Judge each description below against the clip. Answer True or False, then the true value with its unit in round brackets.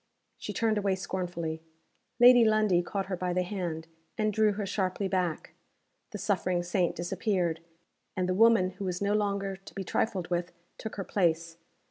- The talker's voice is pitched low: False (190 Hz)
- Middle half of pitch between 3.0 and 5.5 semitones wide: False (2.6 semitones)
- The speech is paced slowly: False (170 wpm)